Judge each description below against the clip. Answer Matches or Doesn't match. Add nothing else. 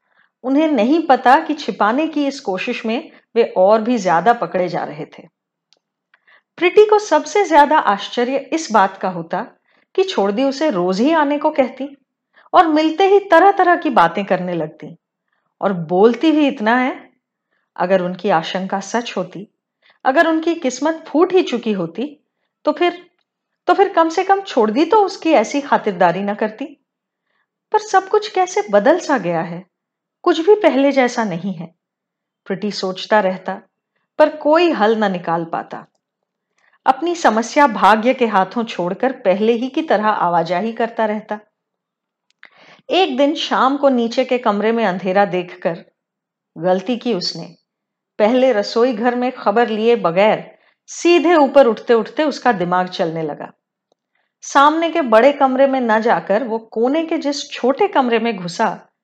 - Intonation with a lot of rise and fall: Matches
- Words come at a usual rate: Matches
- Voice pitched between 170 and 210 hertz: Doesn't match